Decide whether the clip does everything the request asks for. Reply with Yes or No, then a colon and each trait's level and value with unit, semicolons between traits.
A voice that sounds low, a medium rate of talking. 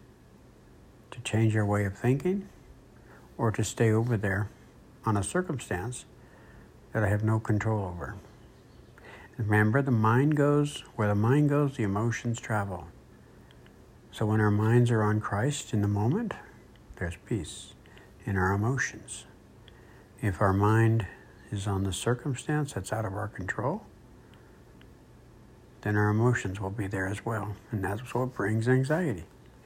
Yes: low, 110 Hz; average, 145 wpm